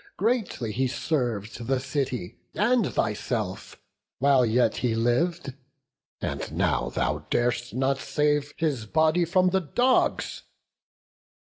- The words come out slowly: Yes, slow, 115 wpm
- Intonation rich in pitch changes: Yes, wide, 5.7 semitones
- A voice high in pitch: No, low, 135 Hz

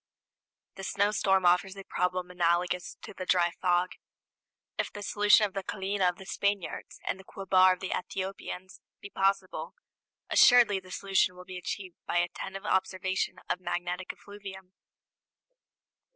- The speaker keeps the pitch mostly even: Yes, narrow, 1.3 semitones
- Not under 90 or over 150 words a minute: Yes, average, 145 wpm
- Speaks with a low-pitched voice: No, high, 190 Hz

